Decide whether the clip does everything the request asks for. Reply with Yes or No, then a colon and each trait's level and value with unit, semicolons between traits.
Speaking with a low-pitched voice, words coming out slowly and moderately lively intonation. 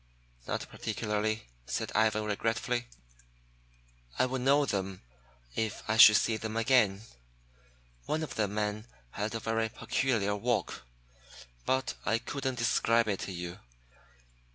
No: low, 110 Hz; slow, 130 wpm; narrow, 2.3 semitones